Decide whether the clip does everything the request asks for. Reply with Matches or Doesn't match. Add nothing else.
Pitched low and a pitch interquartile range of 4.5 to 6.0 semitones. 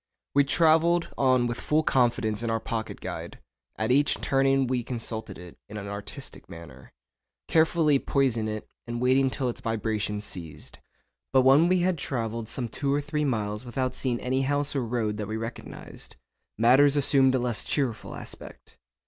Doesn't match